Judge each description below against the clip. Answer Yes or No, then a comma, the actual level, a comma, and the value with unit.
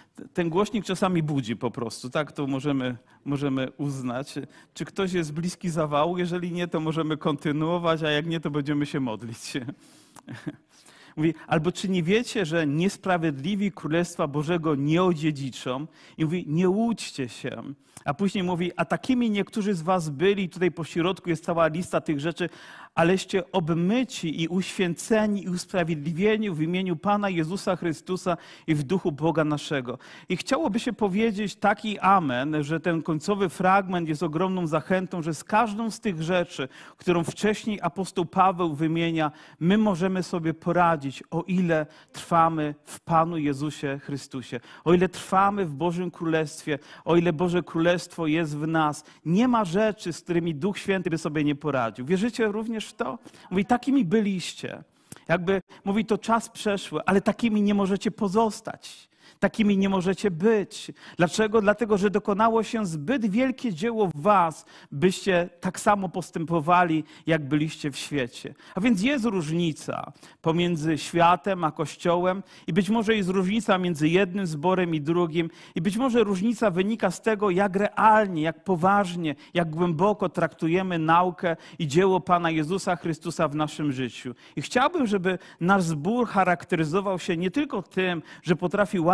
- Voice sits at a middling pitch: Yes, medium, 175 Hz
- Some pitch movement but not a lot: Yes, average, 3.8 semitones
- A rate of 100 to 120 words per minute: No, average, 155 wpm